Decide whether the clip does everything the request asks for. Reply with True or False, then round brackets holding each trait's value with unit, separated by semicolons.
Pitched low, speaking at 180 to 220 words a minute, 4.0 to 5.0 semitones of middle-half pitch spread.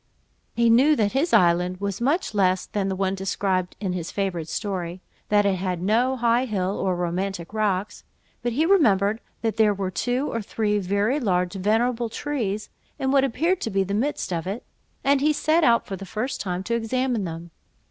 False (205 Hz; 190 wpm; 4.5 semitones)